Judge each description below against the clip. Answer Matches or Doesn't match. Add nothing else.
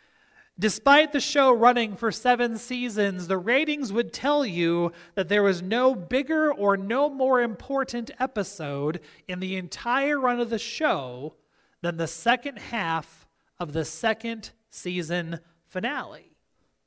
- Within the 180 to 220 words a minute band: Doesn't match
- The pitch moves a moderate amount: Doesn't match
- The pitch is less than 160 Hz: Doesn't match